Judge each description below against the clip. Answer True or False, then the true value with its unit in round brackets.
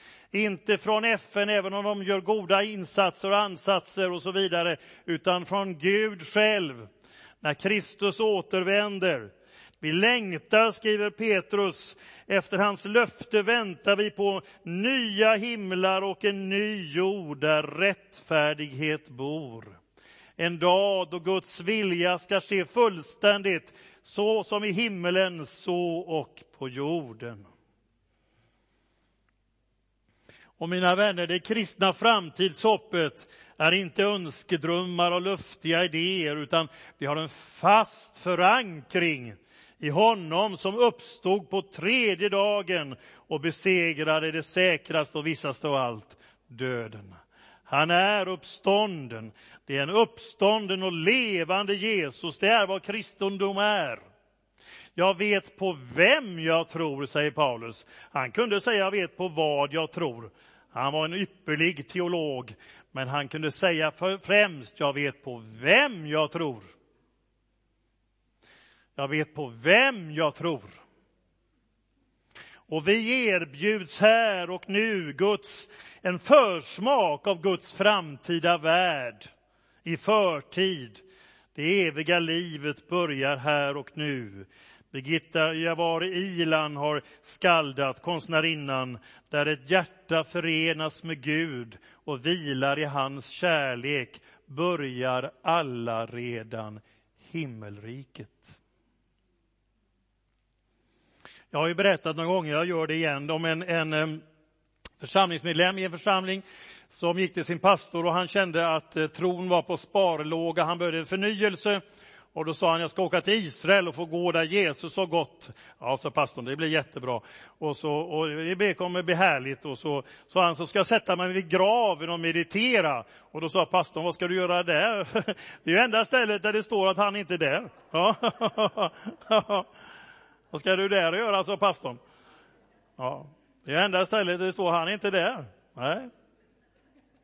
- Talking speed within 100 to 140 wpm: True (135 wpm)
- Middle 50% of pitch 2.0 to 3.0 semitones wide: False (4.7 semitones)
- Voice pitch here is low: False (175 Hz)